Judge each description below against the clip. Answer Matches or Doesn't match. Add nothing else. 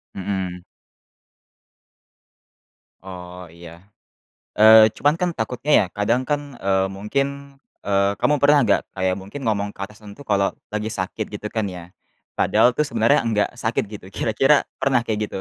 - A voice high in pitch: Doesn't match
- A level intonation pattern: Doesn't match